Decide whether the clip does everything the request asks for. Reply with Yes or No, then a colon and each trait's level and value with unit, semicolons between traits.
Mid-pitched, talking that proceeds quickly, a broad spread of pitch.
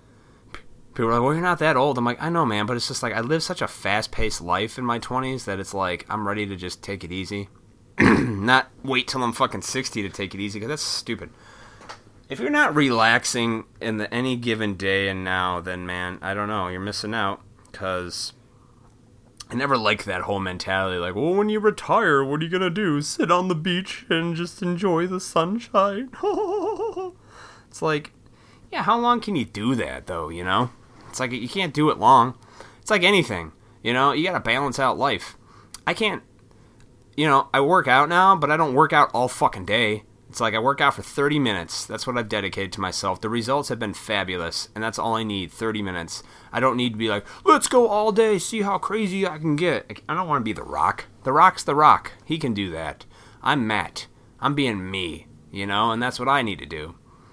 No: low, 120 Hz; fast, 220 wpm; wide, 6.2 semitones